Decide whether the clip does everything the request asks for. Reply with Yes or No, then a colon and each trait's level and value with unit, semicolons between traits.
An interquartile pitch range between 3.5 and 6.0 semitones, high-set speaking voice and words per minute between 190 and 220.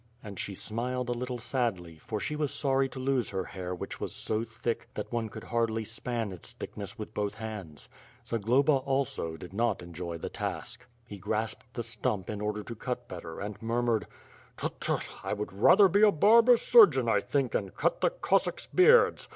No: average, 3.9 semitones; low, 115 Hz; average, 200 wpm